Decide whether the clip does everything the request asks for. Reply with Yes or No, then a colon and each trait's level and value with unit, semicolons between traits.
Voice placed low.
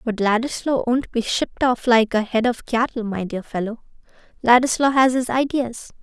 No: high, 240 Hz